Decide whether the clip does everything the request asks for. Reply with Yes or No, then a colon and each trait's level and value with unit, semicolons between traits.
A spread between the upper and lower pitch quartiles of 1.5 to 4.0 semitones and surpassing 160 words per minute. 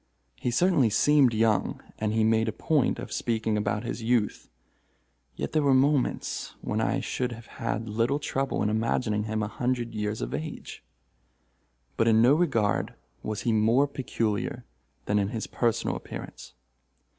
No: average, 3.0 semitones; average, 155 wpm